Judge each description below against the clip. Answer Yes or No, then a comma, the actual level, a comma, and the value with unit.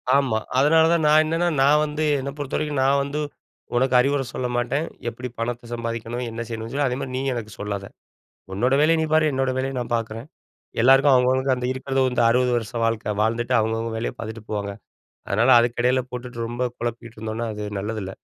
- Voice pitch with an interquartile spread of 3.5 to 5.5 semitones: No, average, 3.0 semitones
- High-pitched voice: No, low, 125 Hz